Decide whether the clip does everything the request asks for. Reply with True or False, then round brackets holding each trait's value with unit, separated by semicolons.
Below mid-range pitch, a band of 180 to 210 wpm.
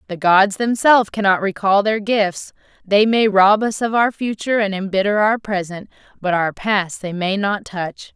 False (200 Hz; 185 wpm)